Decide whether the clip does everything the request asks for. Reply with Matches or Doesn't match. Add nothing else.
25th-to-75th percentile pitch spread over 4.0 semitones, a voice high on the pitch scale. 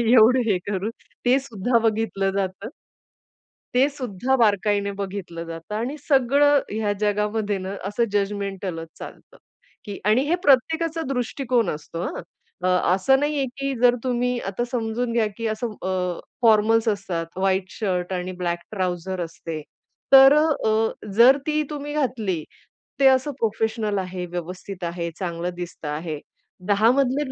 Matches